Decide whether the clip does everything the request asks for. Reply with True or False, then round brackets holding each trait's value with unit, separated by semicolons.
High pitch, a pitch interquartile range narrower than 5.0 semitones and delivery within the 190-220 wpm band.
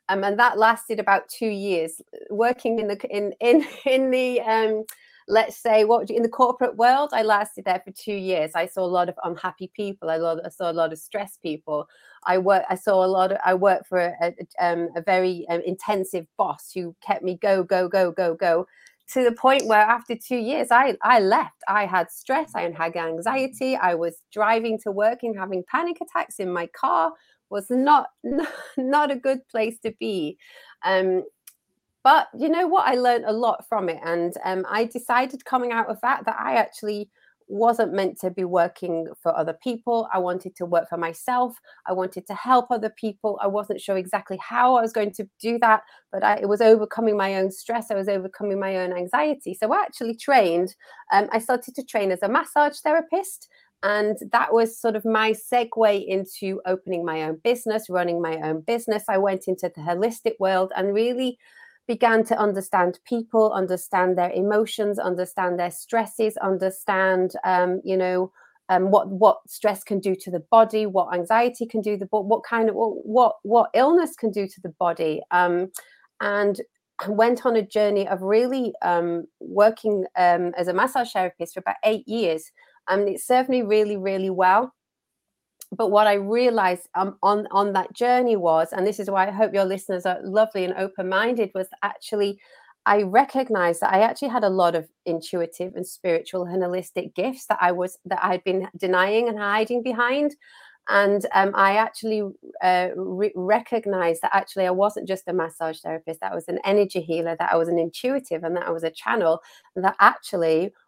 True (200 Hz; 3.8 semitones; 195 wpm)